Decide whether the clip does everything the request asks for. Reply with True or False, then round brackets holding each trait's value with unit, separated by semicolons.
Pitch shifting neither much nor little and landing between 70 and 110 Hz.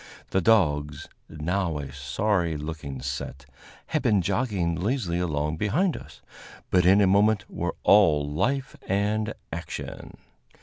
False (5.7 semitones; 90 Hz)